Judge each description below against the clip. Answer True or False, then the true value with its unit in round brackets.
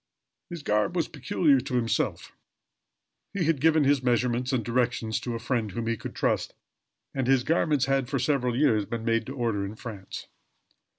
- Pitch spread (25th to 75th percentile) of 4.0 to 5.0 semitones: False (3.4 semitones)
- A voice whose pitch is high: False (125 Hz)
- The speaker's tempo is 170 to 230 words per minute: True (180 wpm)